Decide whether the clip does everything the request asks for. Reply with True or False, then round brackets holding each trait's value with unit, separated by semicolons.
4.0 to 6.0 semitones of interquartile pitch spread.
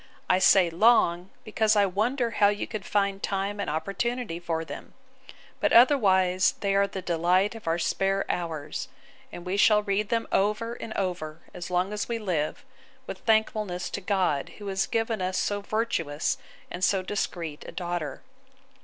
False (3.3 semitones)